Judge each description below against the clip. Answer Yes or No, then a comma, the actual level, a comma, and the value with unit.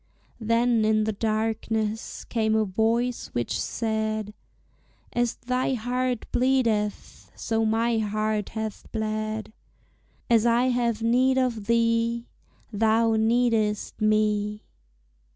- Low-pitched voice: No, high, 225 Hz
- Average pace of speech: No, slow, 105 wpm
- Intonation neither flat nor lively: No, narrow, 1.6 semitones